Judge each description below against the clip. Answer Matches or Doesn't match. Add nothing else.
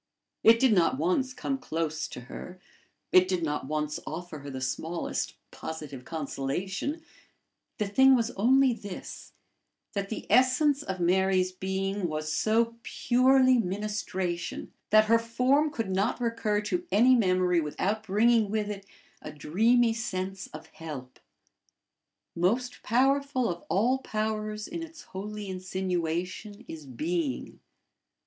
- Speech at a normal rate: Doesn't match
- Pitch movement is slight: Doesn't match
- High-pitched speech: Matches